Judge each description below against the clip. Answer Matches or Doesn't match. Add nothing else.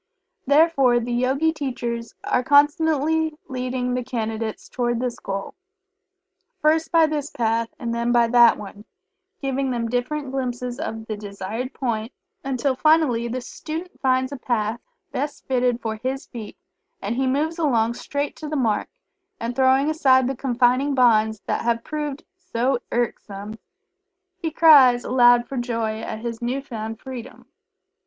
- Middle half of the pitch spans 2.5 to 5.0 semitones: Matches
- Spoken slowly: Doesn't match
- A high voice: Matches